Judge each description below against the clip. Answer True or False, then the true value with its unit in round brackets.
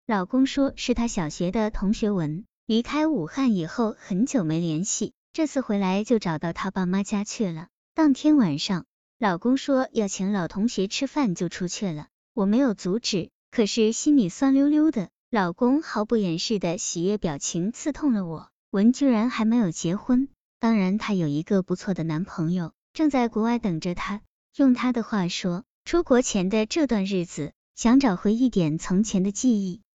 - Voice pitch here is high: True (210 Hz)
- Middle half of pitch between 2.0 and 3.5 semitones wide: False (5.1 semitones)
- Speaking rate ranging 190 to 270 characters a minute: True (260 characters per minute)